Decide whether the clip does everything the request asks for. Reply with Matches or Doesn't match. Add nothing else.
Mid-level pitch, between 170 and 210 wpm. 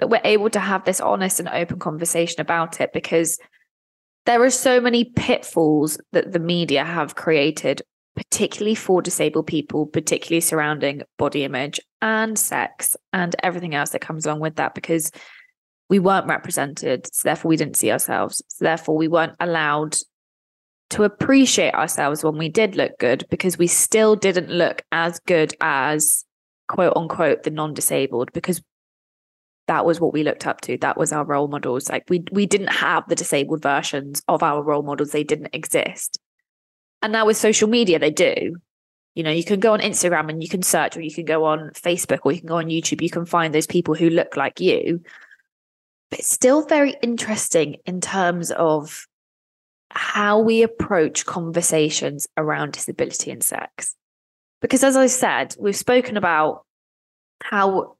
Matches